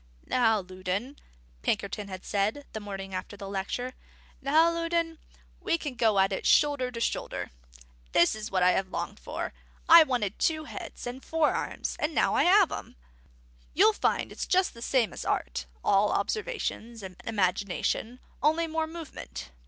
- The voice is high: Yes, high, 235 Hz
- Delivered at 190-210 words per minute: No, average, 165 wpm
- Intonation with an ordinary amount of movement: No, wide, 8.1 semitones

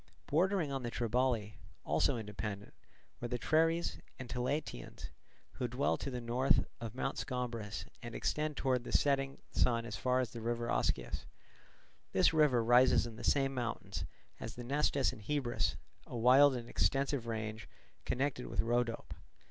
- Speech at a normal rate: Yes, average, 155 wpm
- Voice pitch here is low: Yes, low, 125 Hz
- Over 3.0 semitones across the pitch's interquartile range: No, average, 2.7 semitones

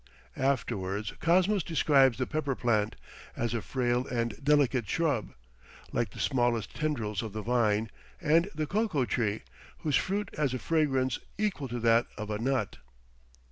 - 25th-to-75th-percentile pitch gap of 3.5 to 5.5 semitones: Yes, average, 4.8 semitones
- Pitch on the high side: No, low, 130 Hz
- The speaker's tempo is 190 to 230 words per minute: No, average, 150 wpm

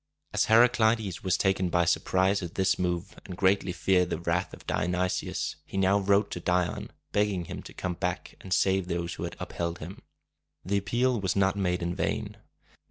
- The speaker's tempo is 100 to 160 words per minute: No, average, 185 wpm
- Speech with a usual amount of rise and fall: No, narrow, 2.0 semitones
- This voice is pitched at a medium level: No, very low, 95 Hz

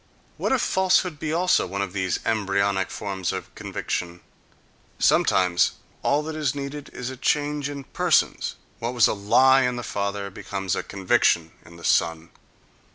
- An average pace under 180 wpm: Yes, average, 160 wpm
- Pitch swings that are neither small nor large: No, wide, 7.0 semitones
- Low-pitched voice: Yes, low, 105 Hz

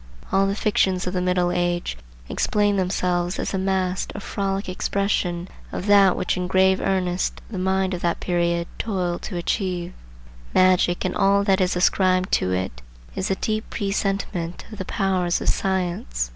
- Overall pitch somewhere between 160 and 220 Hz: Yes, medium, 185 Hz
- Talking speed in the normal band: Yes, average, 170 wpm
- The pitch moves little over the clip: Yes, narrow, 1.7 semitones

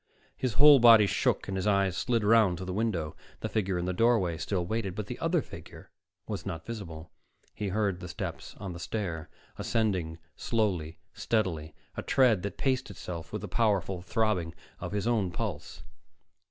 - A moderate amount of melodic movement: Yes, average, 3.9 semitones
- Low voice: Yes, low, 100 Hz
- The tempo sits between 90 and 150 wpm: No, average, 180 wpm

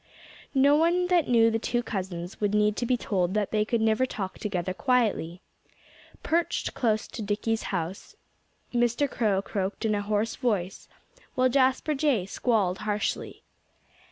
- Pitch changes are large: No, average, 4.0 semitones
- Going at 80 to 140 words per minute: No, average, 155 wpm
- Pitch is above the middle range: Yes, high, 220 Hz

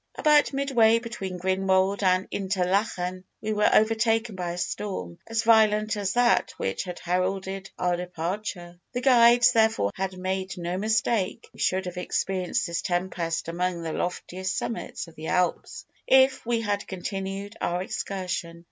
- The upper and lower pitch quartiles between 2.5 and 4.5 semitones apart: Yes, average, 3.4 semitones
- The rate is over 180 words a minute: No, average, 150 wpm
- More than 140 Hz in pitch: Yes, high, 190 Hz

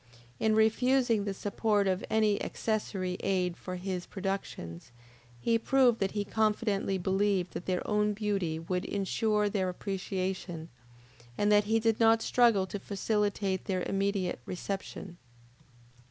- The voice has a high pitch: Yes, high, 200 Hz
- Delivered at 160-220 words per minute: No, slow, 135 wpm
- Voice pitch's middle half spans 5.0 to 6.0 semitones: No, narrow, 2.5 semitones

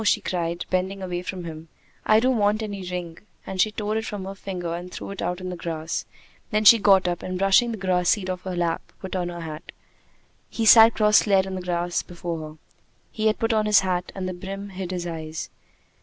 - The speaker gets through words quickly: Yes, fast, 230 wpm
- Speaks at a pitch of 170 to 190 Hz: Yes, medium, 185 Hz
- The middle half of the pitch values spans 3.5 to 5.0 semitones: No, average, 2.7 semitones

